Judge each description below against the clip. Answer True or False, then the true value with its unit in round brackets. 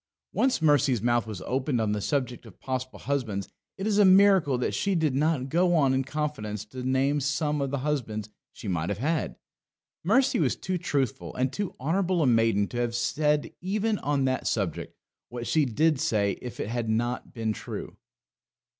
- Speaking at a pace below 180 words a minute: False (190 wpm)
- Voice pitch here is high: False (135 Hz)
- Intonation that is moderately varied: True (5.0 semitones)